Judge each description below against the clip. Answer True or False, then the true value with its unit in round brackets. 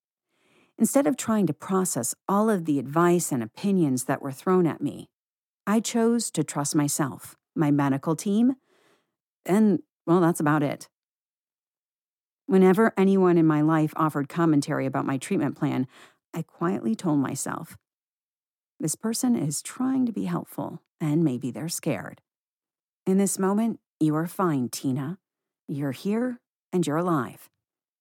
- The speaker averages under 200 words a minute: True (145 wpm)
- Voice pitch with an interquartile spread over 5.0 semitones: True (5.6 semitones)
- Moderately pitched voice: True (165 Hz)